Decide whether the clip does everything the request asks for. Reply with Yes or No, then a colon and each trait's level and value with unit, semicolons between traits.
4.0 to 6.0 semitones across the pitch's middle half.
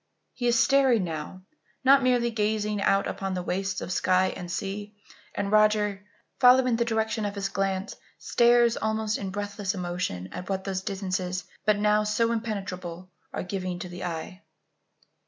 No: average, 2.9 semitones